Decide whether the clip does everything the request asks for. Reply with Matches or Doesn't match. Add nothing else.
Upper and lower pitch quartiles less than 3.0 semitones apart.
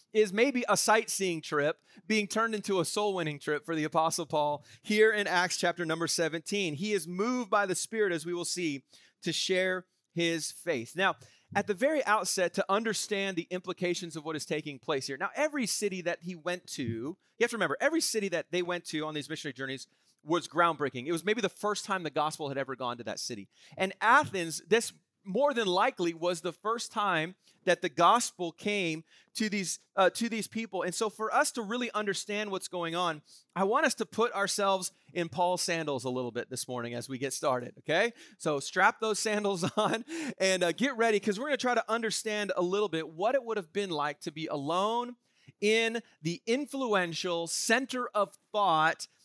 Doesn't match